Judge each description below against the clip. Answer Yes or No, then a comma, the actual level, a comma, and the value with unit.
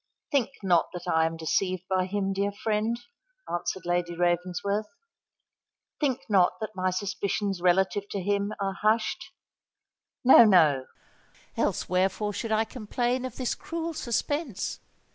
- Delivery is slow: Yes, slow, 130 wpm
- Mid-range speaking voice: No, high, 200 Hz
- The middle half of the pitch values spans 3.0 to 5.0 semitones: Yes, average, 3.3 semitones